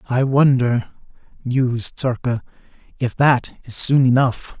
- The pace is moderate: No, slow, 115 wpm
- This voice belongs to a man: Yes, male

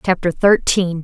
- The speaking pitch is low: No, medium, 180 Hz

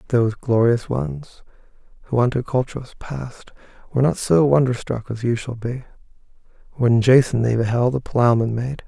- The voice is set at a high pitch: No, low, 125 Hz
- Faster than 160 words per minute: No, average, 155 wpm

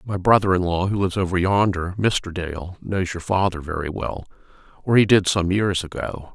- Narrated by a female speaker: No, male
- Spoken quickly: No, average, 190 wpm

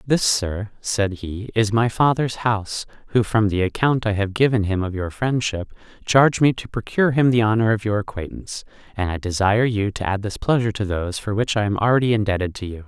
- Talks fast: Yes, fast, 220 wpm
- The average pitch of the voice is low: Yes, low, 110 Hz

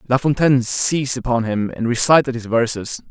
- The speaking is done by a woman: No, male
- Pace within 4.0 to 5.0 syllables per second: No, 5.5 syllables/s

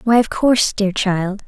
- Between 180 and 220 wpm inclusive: Yes, fast, 205 wpm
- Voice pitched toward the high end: Yes, high, 210 Hz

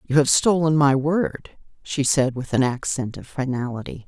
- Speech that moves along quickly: No, average, 175 wpm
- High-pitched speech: No, low, 135 Hz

